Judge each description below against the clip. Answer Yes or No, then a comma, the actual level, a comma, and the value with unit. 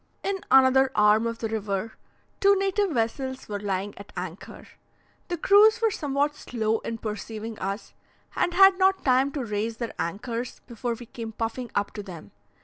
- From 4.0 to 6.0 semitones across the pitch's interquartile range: Yes, average, 5.1 semitones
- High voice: Yes, high, 230 Hz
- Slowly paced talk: No, average, 170 wpm